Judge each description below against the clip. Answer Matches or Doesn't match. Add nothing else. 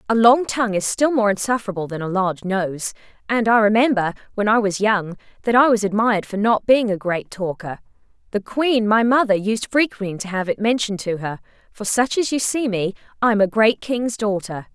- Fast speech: Matches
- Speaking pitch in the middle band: Doesn't match